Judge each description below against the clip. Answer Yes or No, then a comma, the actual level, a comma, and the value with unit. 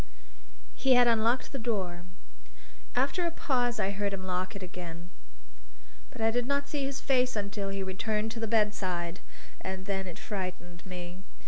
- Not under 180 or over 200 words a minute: No, average, 165 wpm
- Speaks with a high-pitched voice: Yes, high, 205 Hz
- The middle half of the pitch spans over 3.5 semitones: Yes, average, 4.7 semitones